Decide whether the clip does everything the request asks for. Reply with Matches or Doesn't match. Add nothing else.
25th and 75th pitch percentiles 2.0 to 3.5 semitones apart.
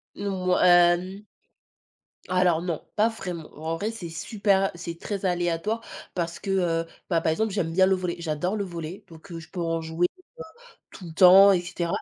Matches